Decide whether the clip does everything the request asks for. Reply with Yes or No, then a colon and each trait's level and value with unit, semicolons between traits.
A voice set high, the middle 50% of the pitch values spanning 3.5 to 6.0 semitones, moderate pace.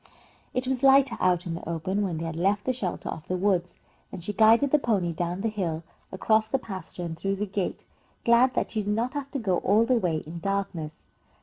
No: high, 195 Hz; average, 4.7 semitones; fast, 230 wpm